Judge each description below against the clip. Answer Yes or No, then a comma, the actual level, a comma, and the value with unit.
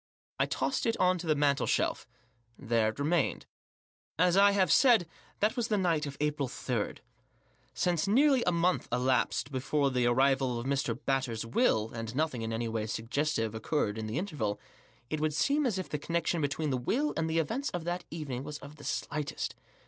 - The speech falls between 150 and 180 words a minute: No, average, 195 wpm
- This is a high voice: No, medium, 150 Hz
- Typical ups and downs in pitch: No, wide, 6.0 semitones